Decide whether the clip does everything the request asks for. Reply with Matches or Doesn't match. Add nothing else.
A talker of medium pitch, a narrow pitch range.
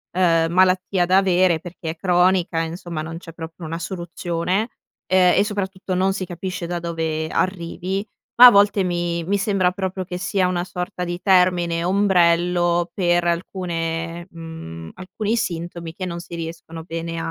Matches